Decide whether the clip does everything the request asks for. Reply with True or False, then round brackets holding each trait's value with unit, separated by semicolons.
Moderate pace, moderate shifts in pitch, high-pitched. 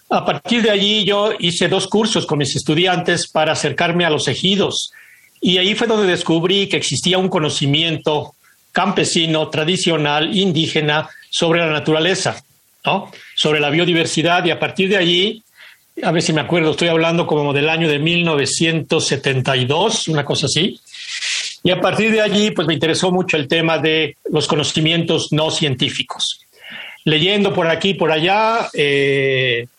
False (155 wpm; 3.4 semitones; 165 Hz)